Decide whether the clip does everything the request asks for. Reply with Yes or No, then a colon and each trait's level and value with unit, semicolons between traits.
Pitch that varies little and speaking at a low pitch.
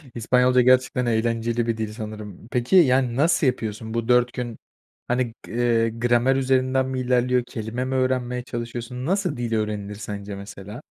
Yes: narrow, 2.2 semitones; low, 120 Hz